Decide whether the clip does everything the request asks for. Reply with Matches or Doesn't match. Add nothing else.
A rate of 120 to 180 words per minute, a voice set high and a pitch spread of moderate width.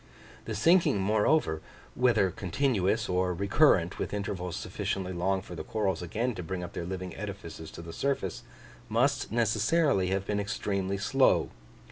Doesn't match